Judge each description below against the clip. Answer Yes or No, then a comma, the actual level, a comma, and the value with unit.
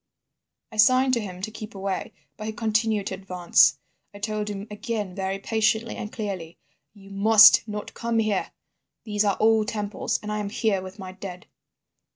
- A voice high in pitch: Yes, high, 210 Hz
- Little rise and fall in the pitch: Yes, narrow, 2.1 semitones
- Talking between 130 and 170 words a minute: No, average, 180 wpm